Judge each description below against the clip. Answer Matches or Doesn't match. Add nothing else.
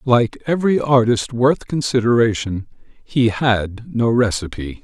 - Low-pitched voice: Matches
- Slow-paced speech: Matches